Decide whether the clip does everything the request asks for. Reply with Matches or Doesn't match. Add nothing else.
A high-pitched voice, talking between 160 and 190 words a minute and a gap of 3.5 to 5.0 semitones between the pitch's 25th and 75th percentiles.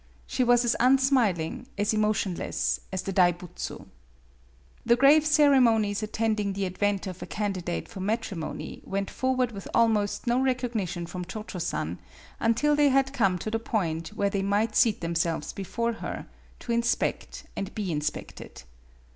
Matches